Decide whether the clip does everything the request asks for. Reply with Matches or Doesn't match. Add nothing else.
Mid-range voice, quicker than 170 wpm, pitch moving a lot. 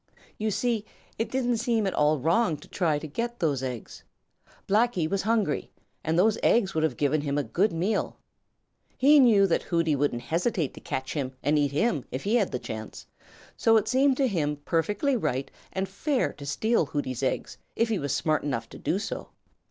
Matches